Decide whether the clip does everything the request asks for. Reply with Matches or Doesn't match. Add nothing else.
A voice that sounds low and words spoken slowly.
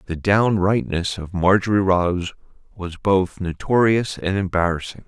Matches